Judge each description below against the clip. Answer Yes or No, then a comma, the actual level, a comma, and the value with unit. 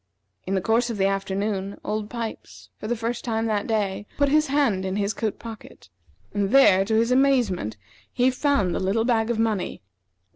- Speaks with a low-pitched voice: No, high, 220 Hz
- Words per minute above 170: Yes, average, 190 wpm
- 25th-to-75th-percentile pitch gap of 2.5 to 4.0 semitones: Yes, average, 3.4 semitones